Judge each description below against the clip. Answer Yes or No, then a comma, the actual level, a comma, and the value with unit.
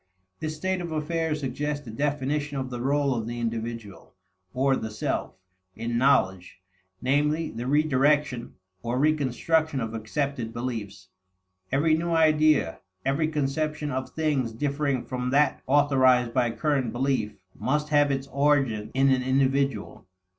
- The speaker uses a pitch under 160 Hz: Yes, low, 135 Hz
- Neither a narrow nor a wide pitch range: Yes, average, 3.7 semitones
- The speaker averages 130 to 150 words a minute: Yes, average, 140 wpm